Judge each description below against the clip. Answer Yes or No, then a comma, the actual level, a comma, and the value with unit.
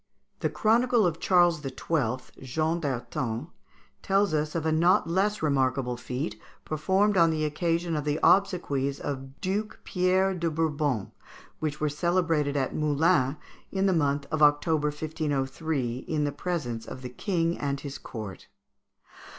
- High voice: No, medium, 155 Hz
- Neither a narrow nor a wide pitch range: Yes, average, 3.9 semitones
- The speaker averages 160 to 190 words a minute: No, average, 145 wpm